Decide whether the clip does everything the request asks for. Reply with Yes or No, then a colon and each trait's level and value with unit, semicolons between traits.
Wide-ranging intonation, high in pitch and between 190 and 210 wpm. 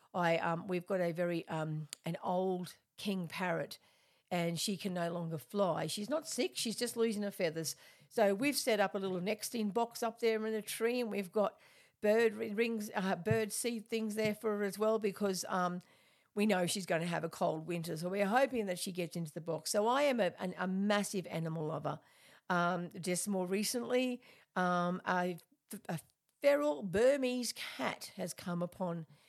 No: average, 4.1 semitones; high, 195 Hz; average, 195 wpm